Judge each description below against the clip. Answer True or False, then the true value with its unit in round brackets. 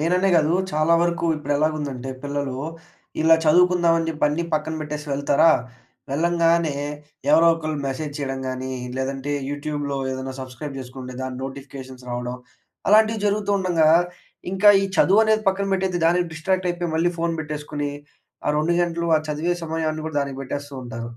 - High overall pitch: False (155 Hz)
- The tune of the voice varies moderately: True (3.7 semitones)